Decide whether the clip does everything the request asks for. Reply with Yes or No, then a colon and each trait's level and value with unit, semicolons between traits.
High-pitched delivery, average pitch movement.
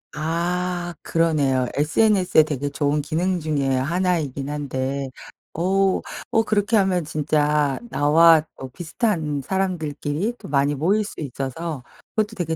No: medium, 160 Hz; average, 4.0 semitones